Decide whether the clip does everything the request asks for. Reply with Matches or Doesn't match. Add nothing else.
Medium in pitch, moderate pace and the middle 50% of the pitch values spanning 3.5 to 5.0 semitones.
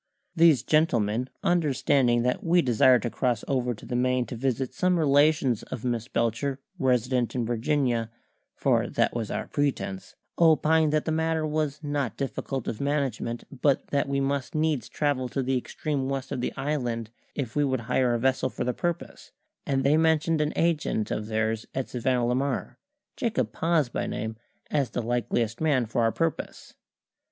Doesn't match